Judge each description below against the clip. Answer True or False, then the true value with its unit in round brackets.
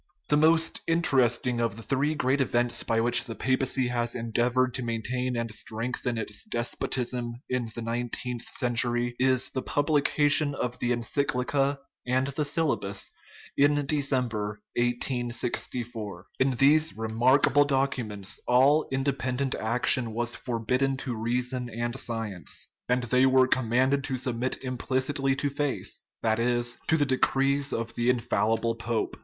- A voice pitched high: False (125 Hz)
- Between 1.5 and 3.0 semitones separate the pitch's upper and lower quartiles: True (2.4 semitones)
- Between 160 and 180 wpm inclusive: False (140 wpm)